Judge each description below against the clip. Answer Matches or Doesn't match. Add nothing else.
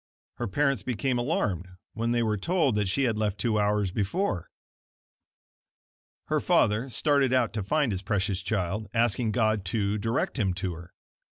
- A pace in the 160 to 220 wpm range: Matches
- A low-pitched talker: Matches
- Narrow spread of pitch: Doesn't match